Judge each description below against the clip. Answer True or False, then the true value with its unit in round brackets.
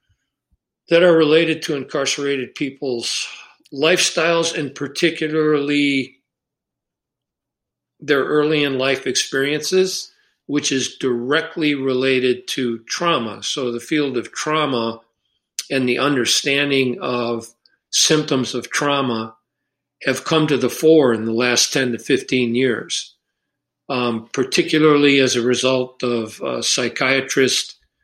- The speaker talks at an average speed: False (110 wpm)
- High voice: False (135 Hz)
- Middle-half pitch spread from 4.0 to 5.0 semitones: False (3.5 semitones)